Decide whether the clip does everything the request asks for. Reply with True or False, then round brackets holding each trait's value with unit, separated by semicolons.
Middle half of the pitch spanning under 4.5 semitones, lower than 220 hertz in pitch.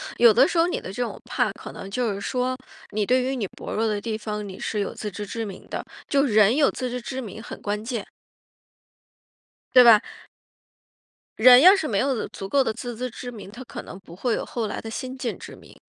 False (3.5 semitones; 230 Hz)